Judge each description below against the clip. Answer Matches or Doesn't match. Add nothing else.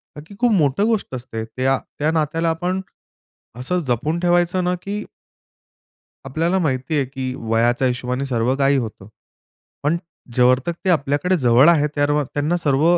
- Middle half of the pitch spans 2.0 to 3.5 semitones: Doesn't match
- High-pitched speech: Doesn't match